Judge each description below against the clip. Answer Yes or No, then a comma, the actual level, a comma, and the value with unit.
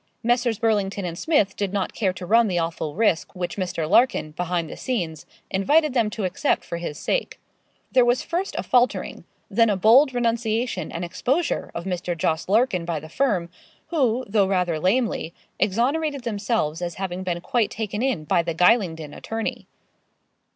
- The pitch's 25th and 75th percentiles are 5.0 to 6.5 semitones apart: Yes, wide, 5.5 semitones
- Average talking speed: Yes, average, 170 wpm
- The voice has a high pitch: Yes, high, 200 Hz